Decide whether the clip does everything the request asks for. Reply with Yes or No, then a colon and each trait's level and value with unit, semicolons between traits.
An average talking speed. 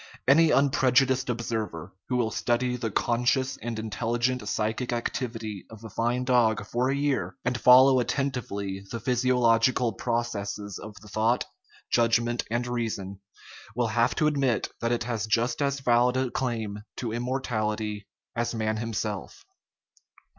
Yes: average, 145 wpm